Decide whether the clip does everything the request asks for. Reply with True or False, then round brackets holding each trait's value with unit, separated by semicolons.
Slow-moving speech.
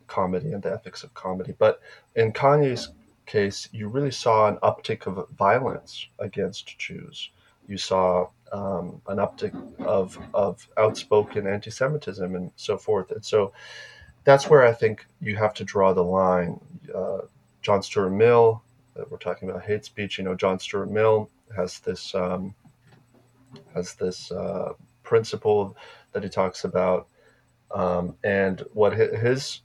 False (145 wpm)